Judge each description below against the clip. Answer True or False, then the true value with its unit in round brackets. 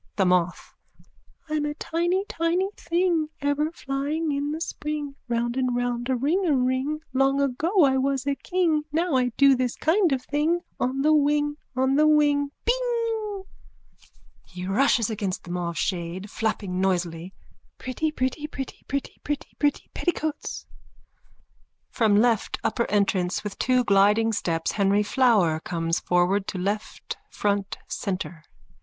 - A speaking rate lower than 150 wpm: True (140 wpm)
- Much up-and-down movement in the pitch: True (6.9 semitones)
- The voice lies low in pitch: False (265 Hz)